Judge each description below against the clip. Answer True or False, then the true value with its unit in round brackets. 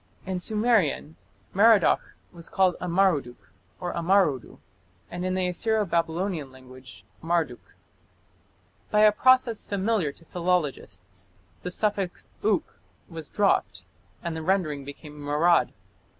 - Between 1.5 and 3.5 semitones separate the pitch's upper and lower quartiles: False (5.0 semitones)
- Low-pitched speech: False (175 Hz)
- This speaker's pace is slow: True (115 wpm)